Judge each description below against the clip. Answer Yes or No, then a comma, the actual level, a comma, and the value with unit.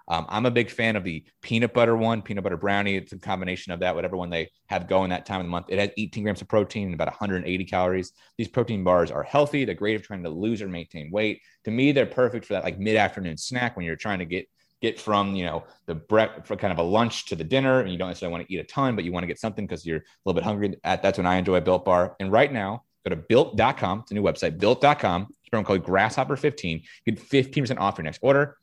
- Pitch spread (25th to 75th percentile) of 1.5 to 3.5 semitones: No, average, 3.9 semitones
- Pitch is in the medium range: No, low, 100 Hz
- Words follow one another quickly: Yes, fast, 275 wpm